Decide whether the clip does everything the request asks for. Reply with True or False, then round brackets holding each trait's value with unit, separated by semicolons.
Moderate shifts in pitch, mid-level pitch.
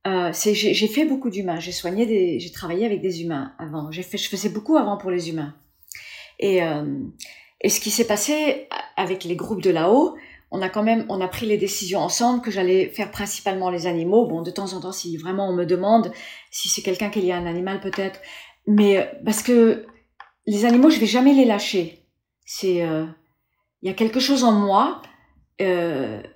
False (3.7 semitones; 195 Hz)